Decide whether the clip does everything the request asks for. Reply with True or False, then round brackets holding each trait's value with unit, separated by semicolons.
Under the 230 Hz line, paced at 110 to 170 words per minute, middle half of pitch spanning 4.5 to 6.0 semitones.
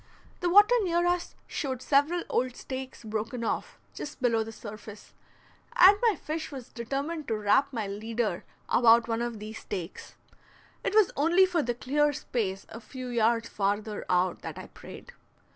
False (240 Hz; 165 wpm; 5.3 semitones)